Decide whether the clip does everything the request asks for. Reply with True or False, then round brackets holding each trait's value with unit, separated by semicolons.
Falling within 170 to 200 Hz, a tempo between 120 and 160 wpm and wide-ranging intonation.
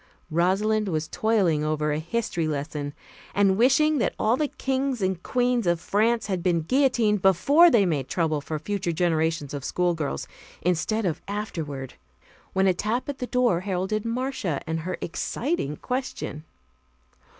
True (190 Hz; 150 wpm; 6.4 semitones)